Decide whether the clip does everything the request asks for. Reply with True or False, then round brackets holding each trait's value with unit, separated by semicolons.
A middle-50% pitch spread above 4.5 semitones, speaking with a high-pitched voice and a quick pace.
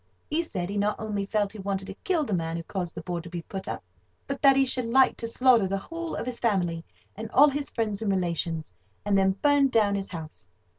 True (5.4 semitones; 205 Hz; 245 wpm)